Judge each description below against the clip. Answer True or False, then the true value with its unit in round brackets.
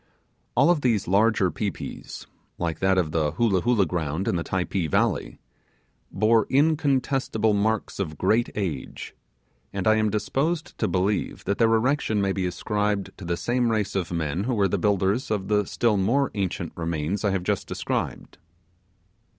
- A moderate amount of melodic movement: True (3.6 semitones)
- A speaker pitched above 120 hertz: False (100 Hz)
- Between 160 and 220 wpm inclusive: True (170 wpm)